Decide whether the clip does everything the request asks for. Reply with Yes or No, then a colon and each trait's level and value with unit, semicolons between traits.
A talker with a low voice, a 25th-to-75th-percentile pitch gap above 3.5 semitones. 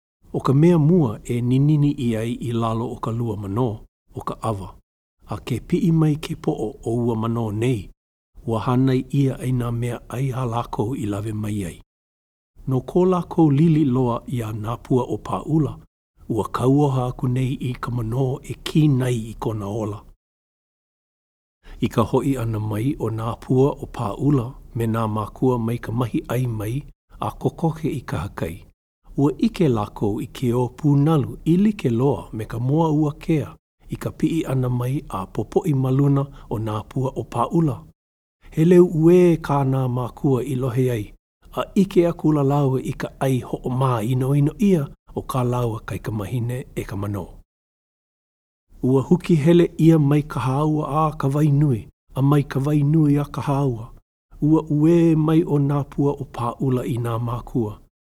Yes: low, 130 Hz; average, 4.2 semitones